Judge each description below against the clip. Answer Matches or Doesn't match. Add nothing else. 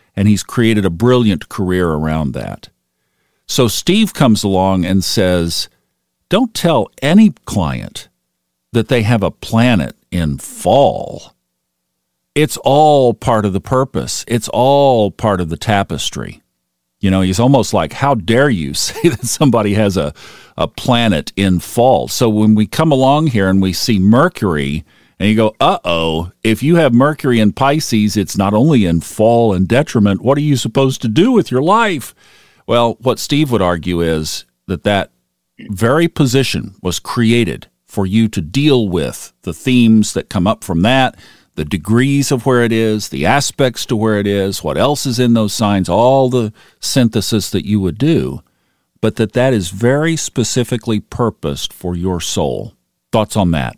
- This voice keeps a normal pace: Matches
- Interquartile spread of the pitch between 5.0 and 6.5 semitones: Matches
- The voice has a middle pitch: Doesn't match